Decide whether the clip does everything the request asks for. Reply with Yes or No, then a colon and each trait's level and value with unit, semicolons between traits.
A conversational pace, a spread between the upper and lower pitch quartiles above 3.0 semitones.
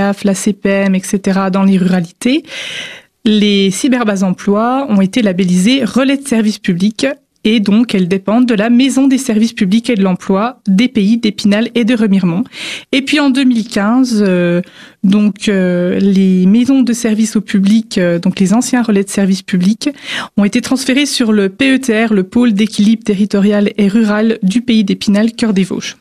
Yes: average, 170 wpm; average, 3.5 semitones